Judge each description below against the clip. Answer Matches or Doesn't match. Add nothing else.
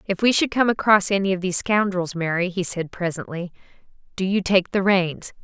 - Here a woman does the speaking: Matches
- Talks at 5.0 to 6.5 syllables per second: Matches